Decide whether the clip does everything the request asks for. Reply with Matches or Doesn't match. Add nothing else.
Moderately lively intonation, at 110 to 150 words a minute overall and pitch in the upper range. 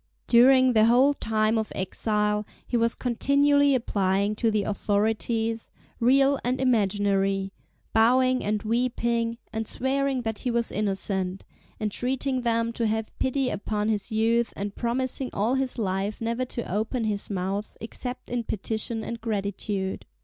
Matches